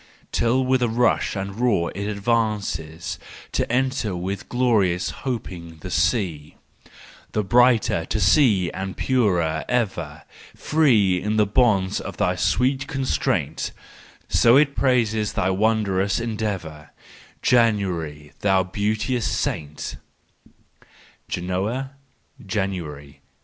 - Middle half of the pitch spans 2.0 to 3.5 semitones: No, average, 4.8 semitones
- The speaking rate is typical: No, slow, 115 wpm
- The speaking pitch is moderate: No, low, 100 Hz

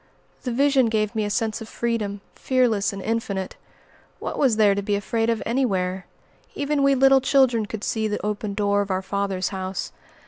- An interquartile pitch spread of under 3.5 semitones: Yes, average, 3.1 semitones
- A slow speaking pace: No, average, 185 wpm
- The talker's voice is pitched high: Yes, high, 215 Hz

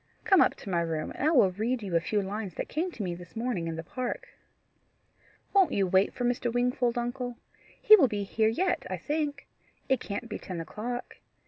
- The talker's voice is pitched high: Yes, high, 235 Hz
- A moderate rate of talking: No, fast, 215 wpm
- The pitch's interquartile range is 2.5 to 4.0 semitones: No, average, 5.0 semitones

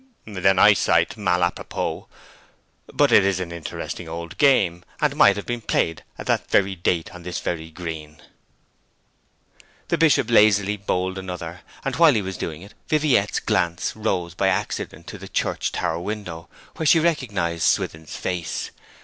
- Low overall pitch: Yes, very low, 95 Hz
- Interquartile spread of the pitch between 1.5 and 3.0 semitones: No, average, 3.9 semitones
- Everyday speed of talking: Yes, average, 165 wpm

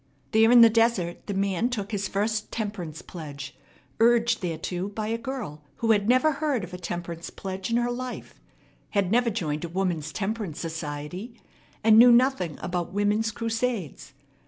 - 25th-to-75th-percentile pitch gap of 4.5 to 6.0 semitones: Yes, average, 4.8 semitones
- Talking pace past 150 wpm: Yes, average, 165 wpm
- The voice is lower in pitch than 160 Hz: No, high, 205 Hz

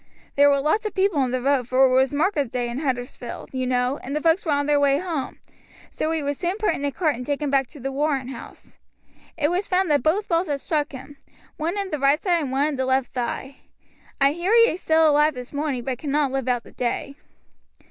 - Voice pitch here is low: No, very high, 285 Hz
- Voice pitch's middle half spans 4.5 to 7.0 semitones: No, average, 3.3 semitones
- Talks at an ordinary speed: No, fast, 250 wpm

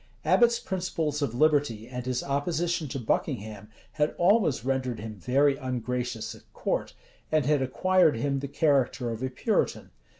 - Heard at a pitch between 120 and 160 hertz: Yes, low, 135 Hz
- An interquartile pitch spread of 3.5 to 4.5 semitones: Yes, average, 3.9 semitones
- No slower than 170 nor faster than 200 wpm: No, average, 160 wpm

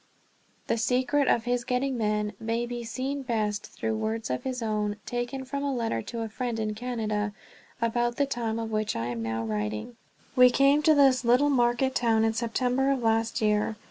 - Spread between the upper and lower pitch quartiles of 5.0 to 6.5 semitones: No, average, 2.7 semitones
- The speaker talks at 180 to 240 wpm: Yes, average, 195 wpm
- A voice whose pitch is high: Yes, high, 235 Hz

